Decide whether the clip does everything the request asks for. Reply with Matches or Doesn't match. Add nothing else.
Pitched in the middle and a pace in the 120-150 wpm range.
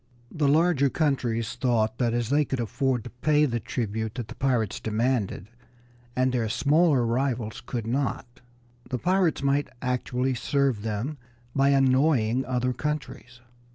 Doesn't match